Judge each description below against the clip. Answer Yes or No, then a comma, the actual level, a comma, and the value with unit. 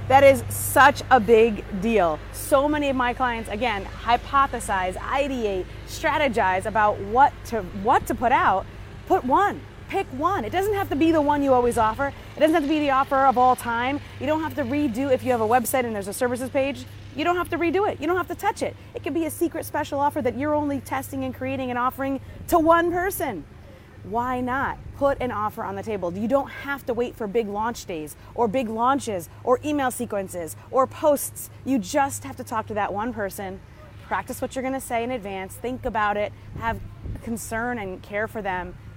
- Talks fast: Yes, fast, 220 wpm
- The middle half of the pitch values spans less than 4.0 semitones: No, average, 4.6 semitones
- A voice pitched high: Yes, very high, 255 Hz